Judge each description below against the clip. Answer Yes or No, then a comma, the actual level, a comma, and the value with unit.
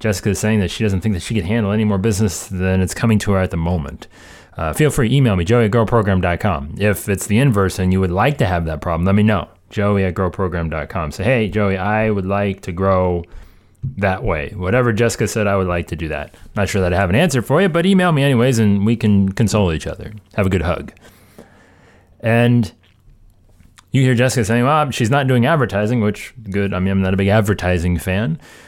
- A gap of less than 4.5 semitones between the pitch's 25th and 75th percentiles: Yes, average, 3.6 semitones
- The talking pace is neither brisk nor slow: No, fast, 225 wpm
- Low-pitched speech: Yes, low, 100 Hz